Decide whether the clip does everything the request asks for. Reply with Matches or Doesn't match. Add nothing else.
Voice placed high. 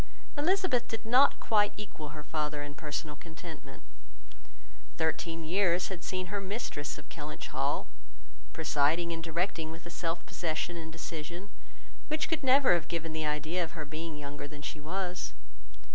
Doesn't match